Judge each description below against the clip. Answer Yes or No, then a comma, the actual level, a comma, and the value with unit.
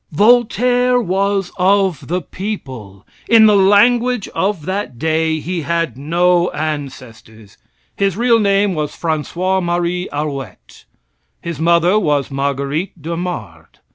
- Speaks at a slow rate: Yes, slow, 115 wpm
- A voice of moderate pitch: Yes, medium, 175 Hz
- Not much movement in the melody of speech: No, average, 5.1 semitones